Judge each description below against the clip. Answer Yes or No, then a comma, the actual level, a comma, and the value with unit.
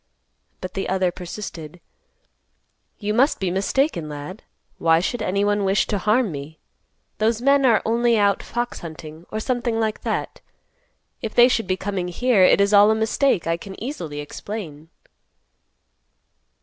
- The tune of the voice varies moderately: Yes, average, 4.4 semitones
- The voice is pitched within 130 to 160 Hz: No, high, 205 Hz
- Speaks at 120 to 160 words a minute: Yes, average, 155 wpm